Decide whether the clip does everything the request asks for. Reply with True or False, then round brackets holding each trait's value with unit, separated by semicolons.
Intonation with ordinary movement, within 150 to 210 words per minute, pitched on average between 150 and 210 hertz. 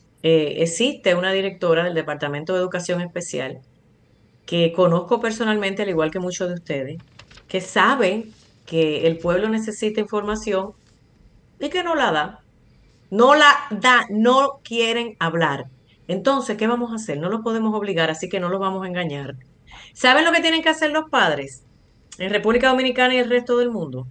False (6.2 semitones; 170 wpm; 190 Hz)